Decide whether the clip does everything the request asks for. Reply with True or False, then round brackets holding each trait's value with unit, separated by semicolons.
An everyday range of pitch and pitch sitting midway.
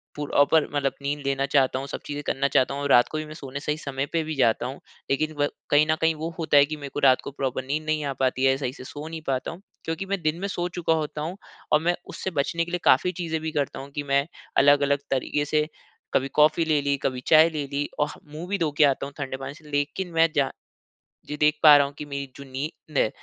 False (2.2 semitones; 145 Hz)